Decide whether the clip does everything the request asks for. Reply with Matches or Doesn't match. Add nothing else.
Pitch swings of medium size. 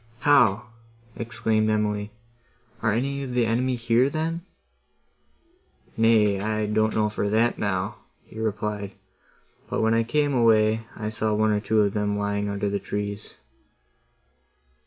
Doesn't match